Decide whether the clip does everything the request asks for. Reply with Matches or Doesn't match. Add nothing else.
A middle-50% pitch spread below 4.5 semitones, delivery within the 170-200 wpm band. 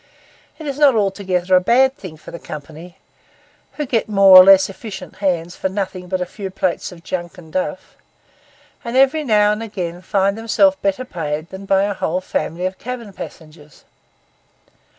Matches